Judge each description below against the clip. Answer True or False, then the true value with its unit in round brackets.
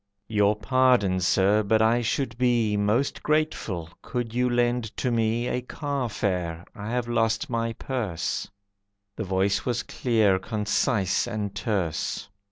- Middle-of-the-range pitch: False (110 Hz)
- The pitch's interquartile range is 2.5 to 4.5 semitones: True (3.2 semitones)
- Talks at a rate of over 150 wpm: False (135 wpm)